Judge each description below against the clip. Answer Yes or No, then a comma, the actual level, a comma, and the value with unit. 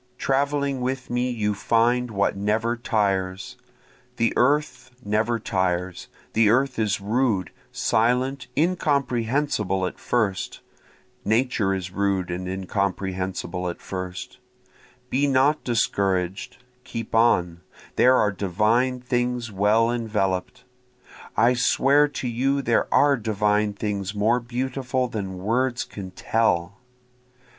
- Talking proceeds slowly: Yes, slow, 115 wpm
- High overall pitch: No, low, 115 Hz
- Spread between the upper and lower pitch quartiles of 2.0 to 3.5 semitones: No, average, 4.4 semitones